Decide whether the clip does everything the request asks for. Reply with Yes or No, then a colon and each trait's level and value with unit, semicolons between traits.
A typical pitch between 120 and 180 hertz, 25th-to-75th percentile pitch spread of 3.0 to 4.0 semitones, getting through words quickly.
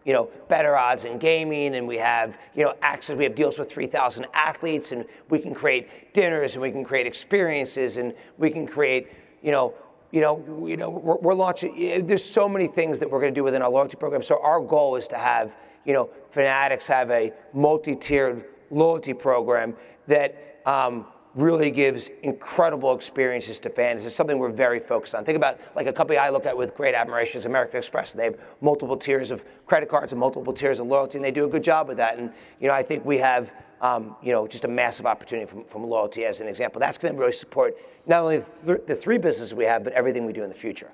Yes: medium, 140 Hz; average, 3.7 semitones; fast, 230 wpm